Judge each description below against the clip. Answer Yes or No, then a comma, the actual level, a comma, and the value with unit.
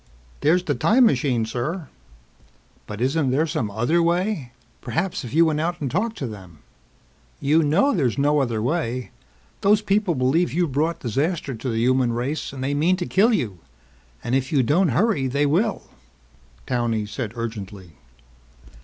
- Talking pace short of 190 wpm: Yes, average, 165 wpm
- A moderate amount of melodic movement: No, wide, 6.1 semitones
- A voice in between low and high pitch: Yes, medium, 145 Hz